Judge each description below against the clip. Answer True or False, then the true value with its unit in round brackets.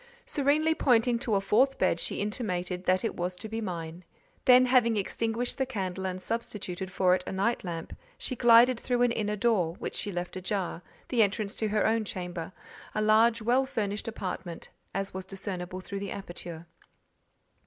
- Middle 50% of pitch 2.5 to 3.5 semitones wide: False (4.1 semitones)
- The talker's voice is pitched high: True (205 Hz)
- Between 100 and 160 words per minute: False (175 wpm)